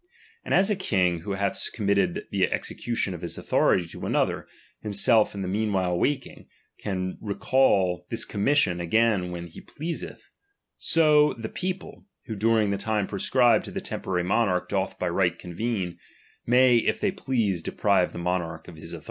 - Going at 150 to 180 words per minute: Yes, average, 170 wpm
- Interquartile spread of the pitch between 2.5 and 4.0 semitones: No, average, 4.5 semitones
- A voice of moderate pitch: No, low, 100 Hz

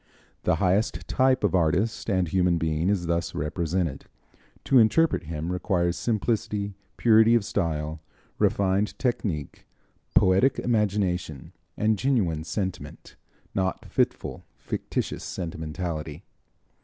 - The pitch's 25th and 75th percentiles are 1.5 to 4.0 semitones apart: No, average, 4.4 semitones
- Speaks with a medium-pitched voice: No, very low, 95 Hz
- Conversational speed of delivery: No, slow, 105 wpm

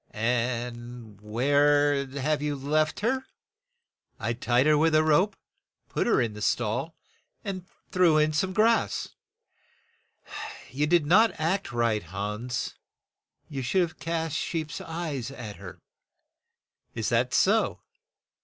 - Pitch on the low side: No, medium, 145 Hz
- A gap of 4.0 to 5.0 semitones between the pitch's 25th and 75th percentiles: No, wide, 5.5 semitones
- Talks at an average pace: No, slow, 125 wpm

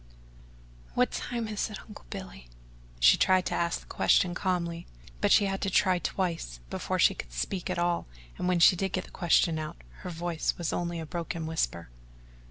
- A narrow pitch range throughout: Yes, narrow, 2.3 semitones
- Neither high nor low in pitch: Yes, medium, 175 Hz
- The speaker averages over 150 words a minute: Yes, average, 190 wpm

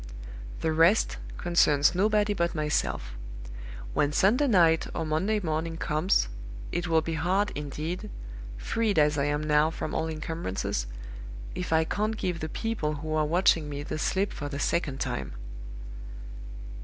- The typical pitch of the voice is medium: Yes, medium, 160 Hz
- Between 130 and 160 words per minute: Yes, average, 150 wpm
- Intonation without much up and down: No, average, 3.3 semitones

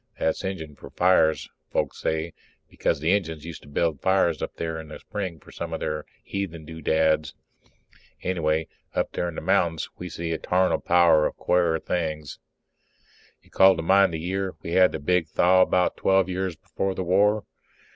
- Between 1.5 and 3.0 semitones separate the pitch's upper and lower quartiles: Yes, average, 2.7 semitones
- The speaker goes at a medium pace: Yes, average, 185 wpm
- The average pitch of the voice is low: Yes, very low, 85 Hz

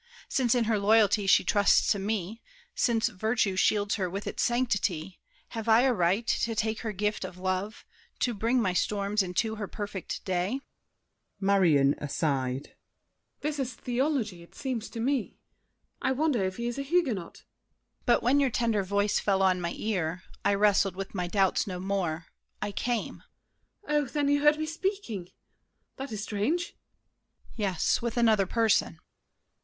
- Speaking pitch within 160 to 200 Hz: No, high, 210 Hz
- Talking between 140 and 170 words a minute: Yes, average, 165 wpm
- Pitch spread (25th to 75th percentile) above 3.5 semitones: Yes, average, 4.1 semitones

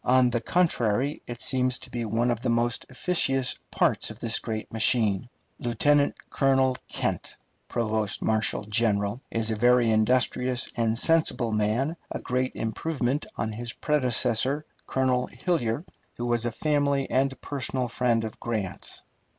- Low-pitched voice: Yes, low, 120 Hz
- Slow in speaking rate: No, average, 145 wpm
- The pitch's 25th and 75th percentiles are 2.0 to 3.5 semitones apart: Yes, average, 2.8 semitones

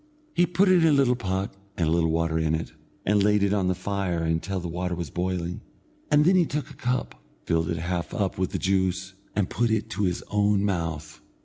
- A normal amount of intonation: Yes, average, 3.6 semitones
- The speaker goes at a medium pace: No, fast, 230 wpm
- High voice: No, very low, 95 Hz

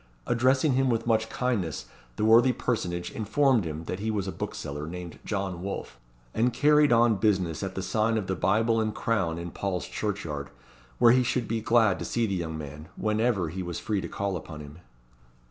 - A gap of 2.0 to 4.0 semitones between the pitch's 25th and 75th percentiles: No, average, 4.8 semitones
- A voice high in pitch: No, low, 105 Hz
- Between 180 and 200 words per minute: Yes, average, 195 wpm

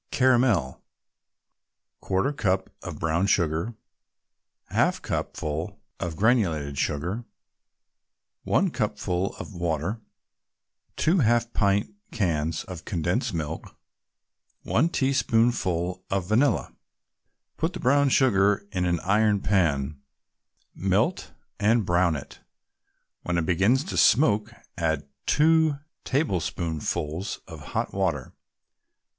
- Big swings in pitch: Yes, wide, 6.1 semitones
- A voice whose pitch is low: Yes, very low, 95 Hz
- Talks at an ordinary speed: No, slow, 100 wpm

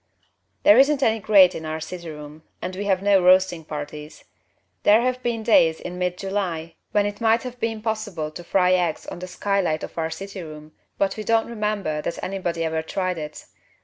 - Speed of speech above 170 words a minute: Yes, average, 200 wpm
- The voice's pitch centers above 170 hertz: Yes, medium, 185 Hz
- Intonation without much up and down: No, average, 4.7 semitones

